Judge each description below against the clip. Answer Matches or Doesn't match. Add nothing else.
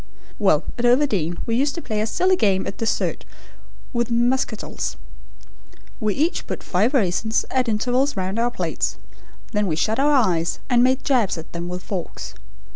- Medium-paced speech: Matches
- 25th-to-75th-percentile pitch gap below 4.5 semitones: Doesn't match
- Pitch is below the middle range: Doesn't match